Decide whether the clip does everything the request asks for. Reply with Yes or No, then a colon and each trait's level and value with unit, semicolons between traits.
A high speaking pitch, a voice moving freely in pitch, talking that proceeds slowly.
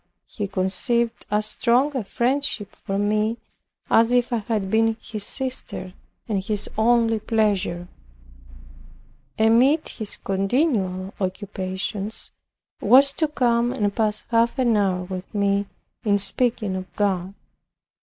No: high, 215 Hz; average, 3.3 semitones; slow, 125 wpm